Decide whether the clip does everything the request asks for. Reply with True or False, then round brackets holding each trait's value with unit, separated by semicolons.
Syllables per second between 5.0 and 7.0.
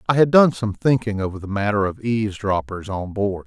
True (5.5 syllables/s)